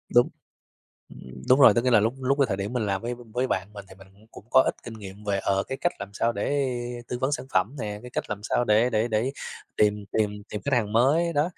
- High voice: No, low, 110 Hz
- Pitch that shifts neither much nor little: Yes, average, 3.9 semitones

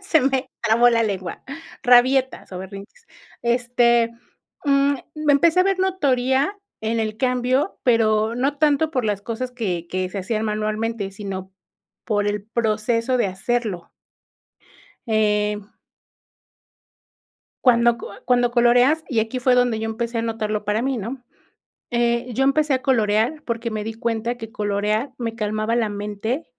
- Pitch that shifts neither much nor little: Yes, average, 3.2 semitones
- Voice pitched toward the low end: No, high, 230 Hz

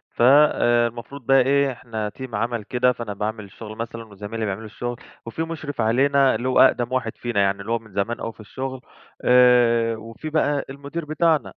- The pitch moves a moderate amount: Yes, average, 3.3 semitones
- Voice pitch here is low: Yes, low, 120 Hz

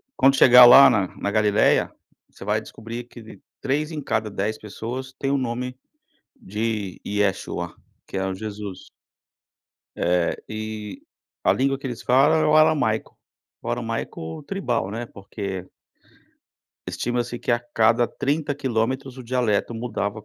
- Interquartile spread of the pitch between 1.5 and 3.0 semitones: No, average, 3.8 semitones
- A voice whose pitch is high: No, low, 115 Hz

